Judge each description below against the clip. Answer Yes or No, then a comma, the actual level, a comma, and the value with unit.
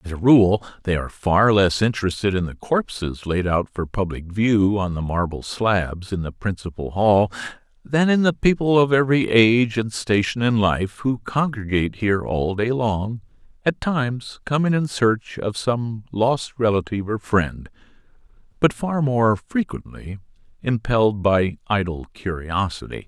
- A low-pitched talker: Yes, low, 110 Hz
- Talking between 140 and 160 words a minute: Yes, average, 155 wpm